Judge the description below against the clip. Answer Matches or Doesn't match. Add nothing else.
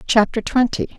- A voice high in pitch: Matches